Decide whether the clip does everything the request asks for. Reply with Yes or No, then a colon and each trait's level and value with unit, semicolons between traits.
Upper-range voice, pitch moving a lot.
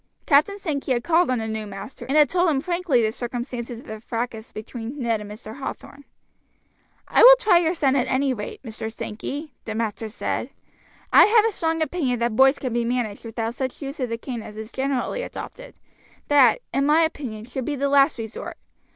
No: very high, 255 Hz; average, 4.7 semitones